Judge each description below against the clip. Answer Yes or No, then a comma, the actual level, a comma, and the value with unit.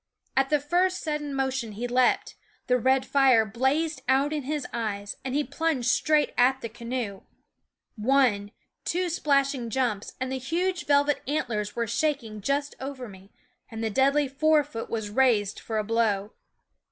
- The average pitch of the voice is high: Yes, very high, 265 Hz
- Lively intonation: No, average, 4.2 semitones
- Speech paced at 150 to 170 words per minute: Yes, average, 165 wpm